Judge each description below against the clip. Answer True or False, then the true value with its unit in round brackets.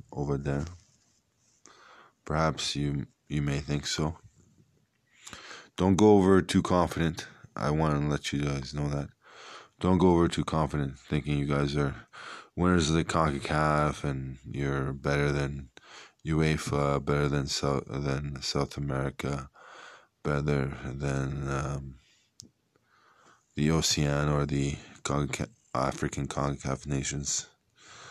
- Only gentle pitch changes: True (2.3 semitones)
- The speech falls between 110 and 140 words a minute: True (120 wpm)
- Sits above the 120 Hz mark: False (70 Hz)